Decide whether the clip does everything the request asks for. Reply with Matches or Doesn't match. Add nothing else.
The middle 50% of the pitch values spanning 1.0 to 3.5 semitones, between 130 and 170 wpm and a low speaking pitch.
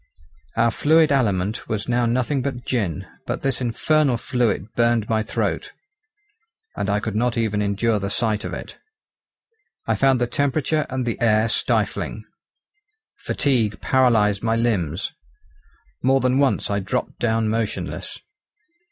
Matches